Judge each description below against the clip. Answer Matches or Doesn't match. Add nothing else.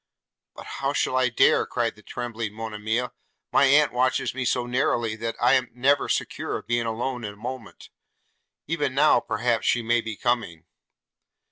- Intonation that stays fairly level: Matches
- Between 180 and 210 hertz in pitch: Doesn't match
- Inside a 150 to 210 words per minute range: Matches